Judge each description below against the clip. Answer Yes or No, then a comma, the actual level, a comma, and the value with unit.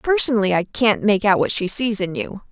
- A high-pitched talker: Yes, high, 205 Hz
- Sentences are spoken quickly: Yes, fast, 240 wpm